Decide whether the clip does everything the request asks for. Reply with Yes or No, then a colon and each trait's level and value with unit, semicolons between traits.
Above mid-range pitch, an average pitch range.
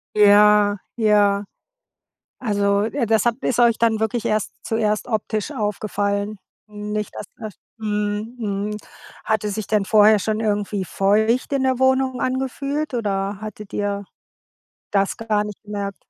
No: high, 210 Hz; narrow, 1.7 semitones